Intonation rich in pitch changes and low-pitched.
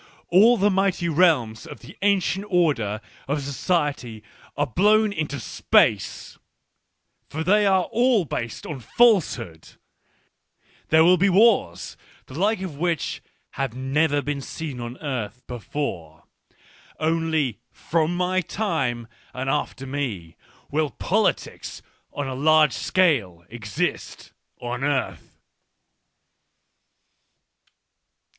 No: wide, 6.7 semitones; medium, 150 Hz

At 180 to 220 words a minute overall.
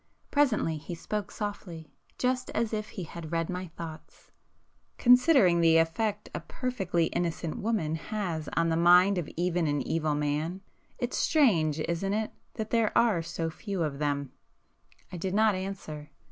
No: average, 160 wpm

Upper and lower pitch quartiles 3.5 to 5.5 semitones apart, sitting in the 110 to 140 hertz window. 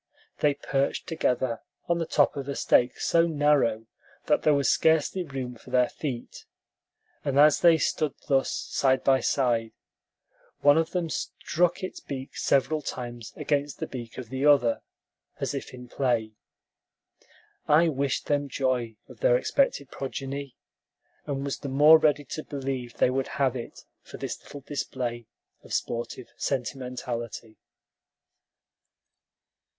No: average, 3.0 semitones; low, 135 Hz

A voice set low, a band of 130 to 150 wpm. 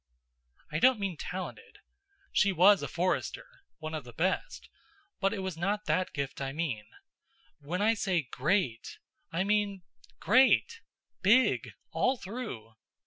No: medium, 185 Hz; average, 140 wpm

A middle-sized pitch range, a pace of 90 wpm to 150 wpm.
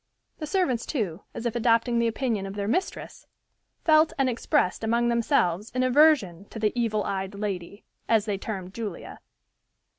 No: average, 4.0 semitones; average, 160 wpm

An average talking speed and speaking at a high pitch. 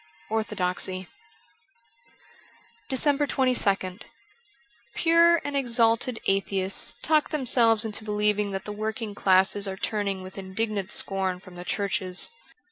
No: slow, 115 wpm; high, 210 Hz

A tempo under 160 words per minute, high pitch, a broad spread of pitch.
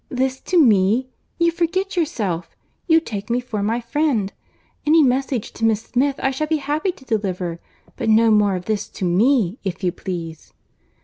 No: average, 170 wpm; high, 235 Hz; wide, 6.4 semitones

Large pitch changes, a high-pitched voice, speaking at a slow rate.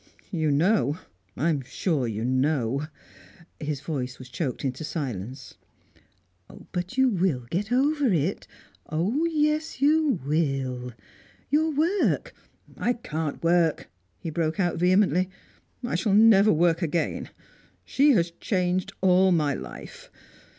No: wide, 6.8 semitones; medium, 170 Hz; slow, 130 wpm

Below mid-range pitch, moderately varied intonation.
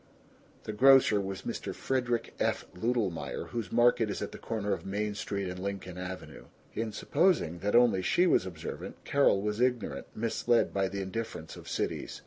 Yes: low, 105 Hz; average, 3.8 semitones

